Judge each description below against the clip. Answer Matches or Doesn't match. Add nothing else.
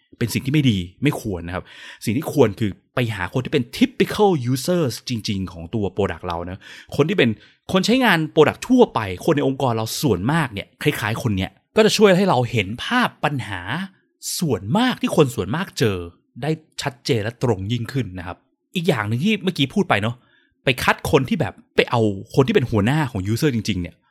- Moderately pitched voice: Doesn't match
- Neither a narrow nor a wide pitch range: Doesn't match